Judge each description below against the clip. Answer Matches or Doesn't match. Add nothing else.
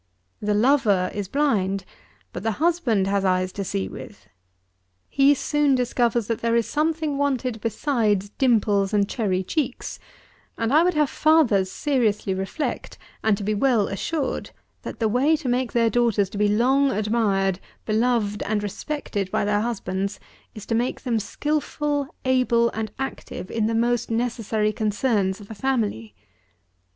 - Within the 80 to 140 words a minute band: Doesn't match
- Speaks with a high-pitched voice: Matches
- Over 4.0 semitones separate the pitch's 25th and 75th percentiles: Matches